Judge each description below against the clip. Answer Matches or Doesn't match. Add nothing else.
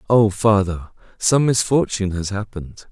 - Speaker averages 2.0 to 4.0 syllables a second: Doesn't match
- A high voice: Doesn't match